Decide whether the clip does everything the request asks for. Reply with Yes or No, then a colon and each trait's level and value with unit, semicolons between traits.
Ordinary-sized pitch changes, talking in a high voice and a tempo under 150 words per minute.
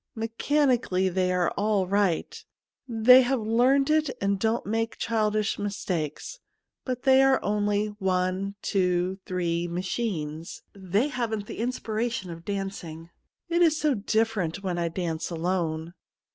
Yes: average, 4.3 semitones; high, 205 Hz; average, 140 wpm